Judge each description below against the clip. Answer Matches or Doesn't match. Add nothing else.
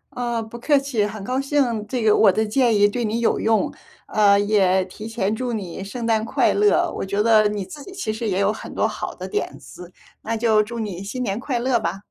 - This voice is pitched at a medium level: Doesn't match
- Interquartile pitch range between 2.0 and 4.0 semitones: Matches